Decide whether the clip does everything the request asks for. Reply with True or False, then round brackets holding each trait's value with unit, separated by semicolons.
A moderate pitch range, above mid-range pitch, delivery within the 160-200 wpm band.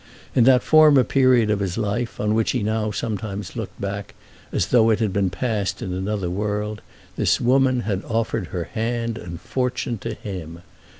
False (3.4 semitones; 110 Hz; 180 wpm)